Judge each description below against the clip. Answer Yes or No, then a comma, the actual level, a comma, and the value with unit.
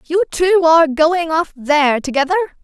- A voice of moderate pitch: No, very high, 320 Hz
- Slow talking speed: No, average, 160 wpm